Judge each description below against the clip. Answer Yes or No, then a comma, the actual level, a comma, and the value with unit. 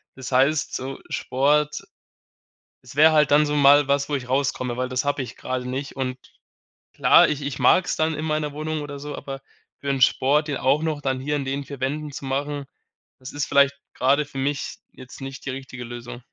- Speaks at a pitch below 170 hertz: Yes, medium, 140 Hz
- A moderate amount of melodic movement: No, narrow, 2.0 semitones